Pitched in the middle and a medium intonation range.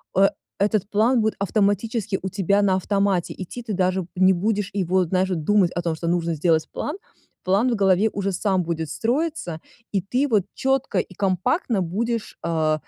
No: high, 195 Hz; average, 3.1 semitones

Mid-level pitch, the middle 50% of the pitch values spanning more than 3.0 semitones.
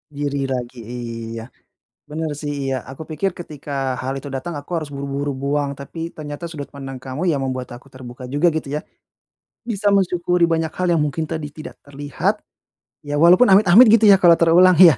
Yes: medium, 145 Hz; average, 3.8 semitones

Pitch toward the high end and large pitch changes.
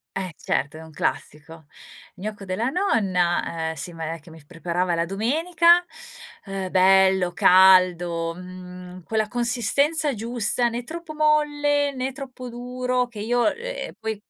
Yes: high, 210 Hz; wide, 6.2 semitones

